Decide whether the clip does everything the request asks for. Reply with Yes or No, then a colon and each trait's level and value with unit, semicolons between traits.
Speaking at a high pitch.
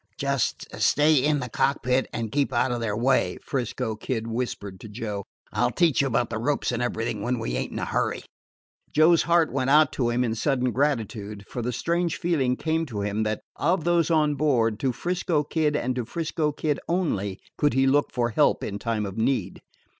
No: low, 130 Hz